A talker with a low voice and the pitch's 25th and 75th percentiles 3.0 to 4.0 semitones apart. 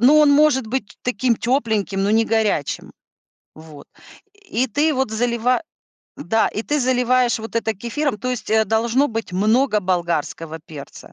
No: high, 225 Hz; average, 3.6 semitones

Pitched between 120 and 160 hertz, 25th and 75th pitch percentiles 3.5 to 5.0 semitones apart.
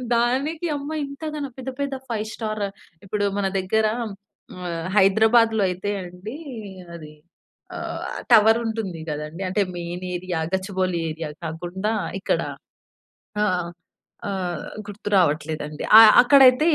No: high, 205 Hz; average, 4.6 semitones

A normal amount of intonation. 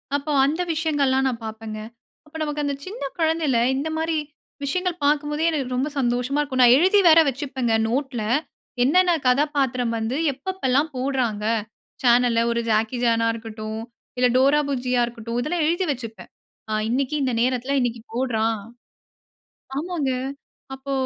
Yes: average, 3.8 semitones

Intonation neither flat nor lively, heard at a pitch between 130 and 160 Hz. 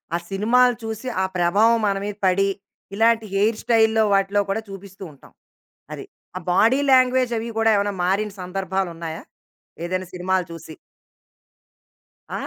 No: average, 3.2 semitones; high, 200 Hz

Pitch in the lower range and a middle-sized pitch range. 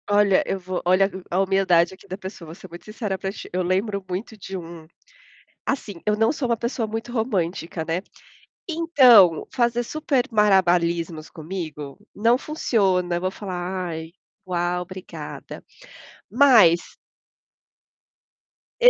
No: high, 190 Hz; average, 4.2 semitones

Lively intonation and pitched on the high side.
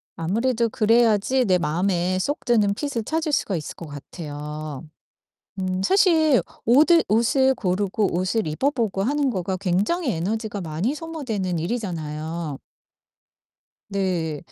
Yes: wide, 6.3 semitones; high, 200 Hz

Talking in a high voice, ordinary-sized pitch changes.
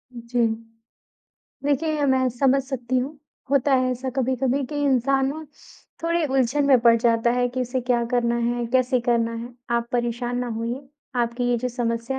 No: very high, 250 Hz; narrow, 2.1 semitones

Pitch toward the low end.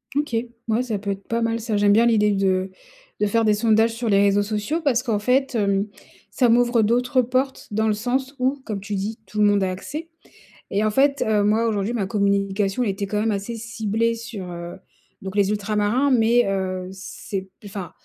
No: high, 215 Hz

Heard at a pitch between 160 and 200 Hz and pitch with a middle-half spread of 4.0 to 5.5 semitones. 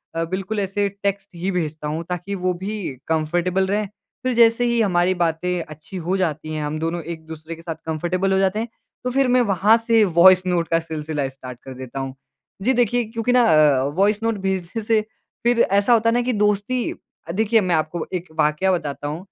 Yes: medium, 185 Hz; average, 4.9 semitones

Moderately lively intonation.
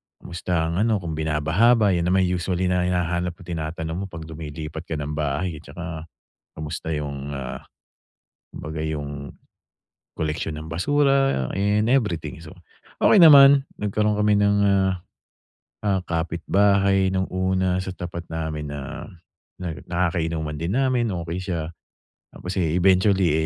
Yes: average, 3.6 semitones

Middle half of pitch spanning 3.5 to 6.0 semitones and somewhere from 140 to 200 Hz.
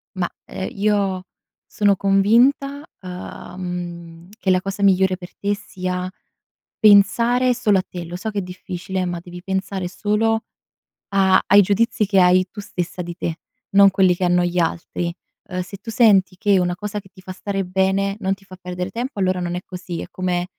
No: narrow, 2.0 semitones; high, 190 Hz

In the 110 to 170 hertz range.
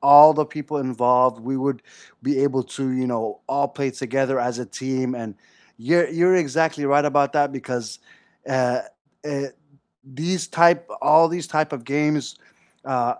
Yes: medium, 140 Hz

